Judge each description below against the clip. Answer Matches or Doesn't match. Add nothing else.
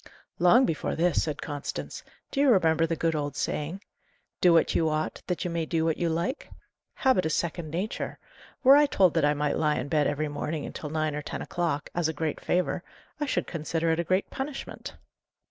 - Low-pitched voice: Doesn't match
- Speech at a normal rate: Doesn't match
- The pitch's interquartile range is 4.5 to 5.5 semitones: Doesn't match